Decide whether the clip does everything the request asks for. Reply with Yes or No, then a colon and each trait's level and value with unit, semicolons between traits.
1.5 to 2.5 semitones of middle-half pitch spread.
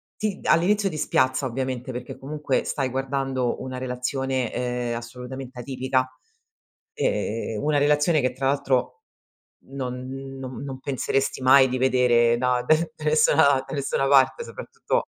Yes: narrow, 2.0 semitones